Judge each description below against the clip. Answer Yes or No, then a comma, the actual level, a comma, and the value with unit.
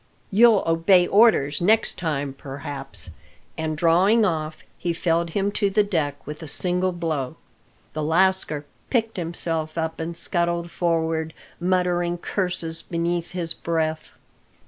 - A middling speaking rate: No, slow, 130 wpm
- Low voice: No, medium, 170 Hz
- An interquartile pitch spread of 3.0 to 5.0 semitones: No, narrow, 2.4 semitones